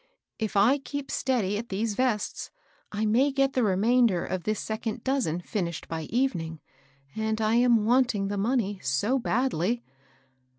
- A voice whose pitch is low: No, high, 220 Hz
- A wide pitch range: No, average, 4.1 semitones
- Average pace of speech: Yes, average, 165 wpm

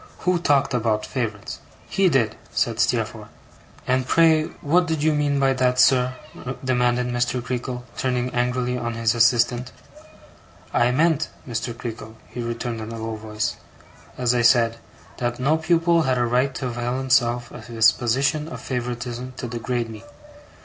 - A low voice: Yes, low, 125 Hz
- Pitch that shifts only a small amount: Yes, narrow, 2.1 semitones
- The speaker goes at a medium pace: Yes, average, 160 wpm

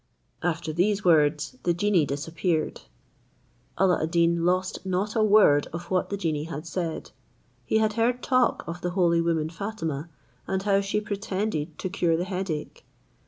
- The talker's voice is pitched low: No, medium, 175 Hz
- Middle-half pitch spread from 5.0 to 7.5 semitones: No, average, 3.5 semitones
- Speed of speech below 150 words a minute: No, average, 165 wpm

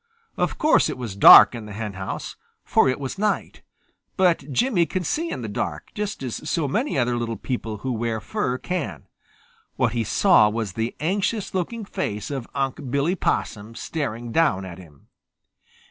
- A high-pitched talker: No, low, 130 Hz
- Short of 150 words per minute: No, average, 175 wpm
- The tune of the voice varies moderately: No, wide, 7.8 semitones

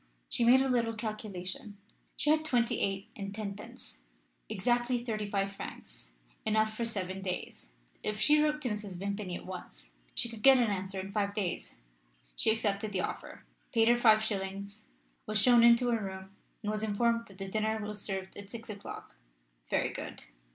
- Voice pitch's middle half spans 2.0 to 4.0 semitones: Yes, average, 3.0 semitones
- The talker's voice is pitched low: No, high, 210 Hz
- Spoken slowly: No, average, 180 wpm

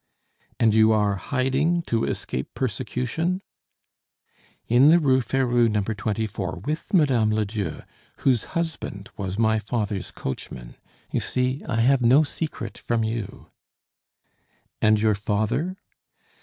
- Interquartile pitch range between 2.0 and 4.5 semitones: Yes, average, 4.0 semitones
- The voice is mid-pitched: No, low, 115 Hz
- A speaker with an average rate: No, slow, 120 wpm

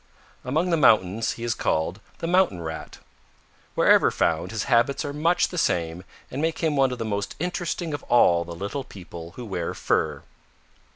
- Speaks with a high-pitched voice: No, low, 115 Hz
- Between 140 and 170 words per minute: No, average, 180 wpm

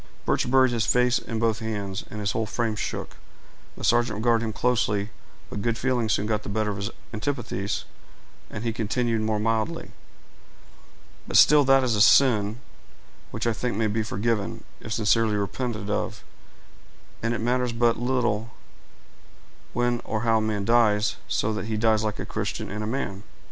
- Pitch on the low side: Yes, low, 110 Hz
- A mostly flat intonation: Yes, narrow, 2.1 semitones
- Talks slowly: No, average, 180 wpm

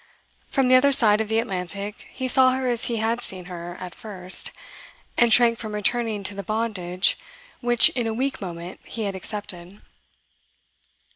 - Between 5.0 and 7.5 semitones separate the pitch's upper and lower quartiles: No, average, 4.2 semitones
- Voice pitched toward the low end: No, high, 215 Hz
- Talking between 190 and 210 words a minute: No, average, 170 wpm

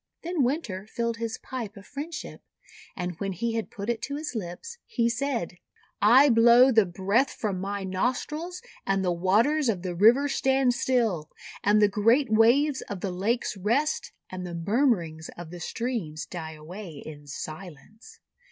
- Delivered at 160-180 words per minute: Yes, average, 170 wpm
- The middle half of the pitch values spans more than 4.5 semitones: Yes, wide, 5.6 semitones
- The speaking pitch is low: No, high, 220 Hz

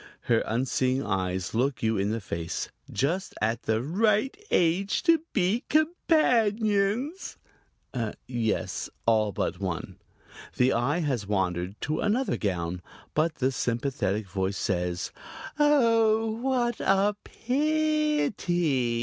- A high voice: No, medium, 140 Hz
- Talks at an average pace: No, slow, 115 wpm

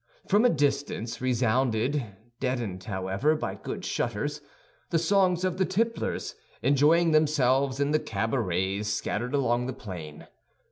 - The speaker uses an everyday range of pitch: No, wide, 5.7 semitones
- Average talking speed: No, slow, 130 wpm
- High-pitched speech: No, low, 130 Hz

